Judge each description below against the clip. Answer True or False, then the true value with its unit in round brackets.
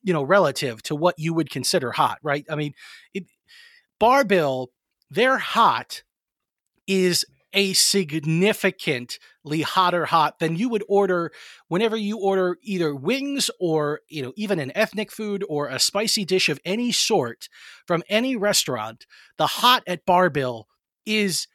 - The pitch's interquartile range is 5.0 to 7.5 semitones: True (5.4 semitones)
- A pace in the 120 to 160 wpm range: True (140 wpm)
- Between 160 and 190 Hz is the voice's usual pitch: True (185 Hz)